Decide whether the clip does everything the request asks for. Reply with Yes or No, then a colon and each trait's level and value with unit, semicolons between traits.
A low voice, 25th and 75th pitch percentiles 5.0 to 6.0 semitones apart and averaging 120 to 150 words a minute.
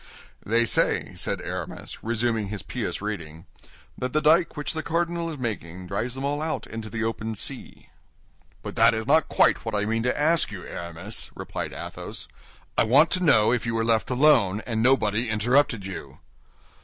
No: low, 115 Hz; average, 5.3 semitones; average, 180 wpm